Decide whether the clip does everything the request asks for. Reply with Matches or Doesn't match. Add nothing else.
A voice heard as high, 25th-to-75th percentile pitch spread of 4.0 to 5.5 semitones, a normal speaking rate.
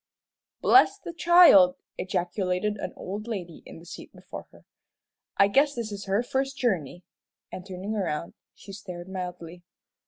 Matches